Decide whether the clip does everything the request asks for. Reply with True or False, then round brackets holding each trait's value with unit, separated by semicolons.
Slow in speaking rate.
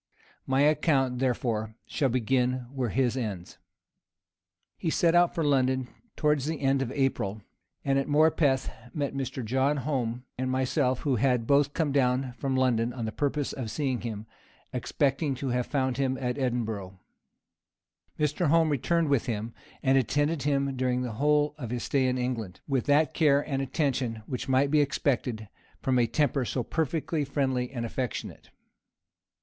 False (165 wpm)